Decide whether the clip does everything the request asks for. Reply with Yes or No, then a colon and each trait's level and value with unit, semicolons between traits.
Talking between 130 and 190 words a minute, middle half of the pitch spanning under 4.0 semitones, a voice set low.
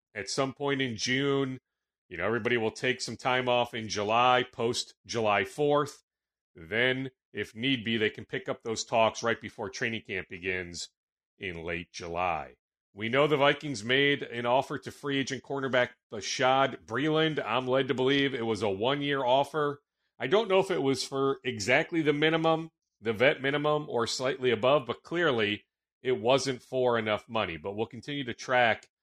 Yes: average, 180 wpm; average, 3.6 semitones; low, 130 Hz